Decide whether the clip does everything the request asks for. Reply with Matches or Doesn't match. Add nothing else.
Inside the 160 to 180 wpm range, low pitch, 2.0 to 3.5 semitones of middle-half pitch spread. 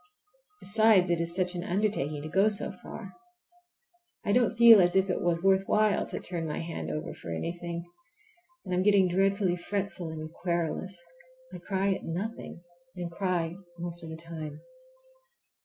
Doesn't match